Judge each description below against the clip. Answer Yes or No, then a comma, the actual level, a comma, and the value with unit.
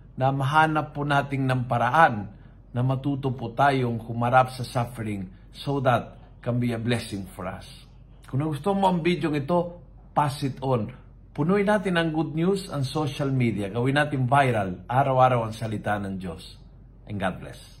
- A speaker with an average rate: No, fast, 165 wpm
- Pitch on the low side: Yes, low, 130 Hz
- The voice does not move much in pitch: No, average, 3.4 semitones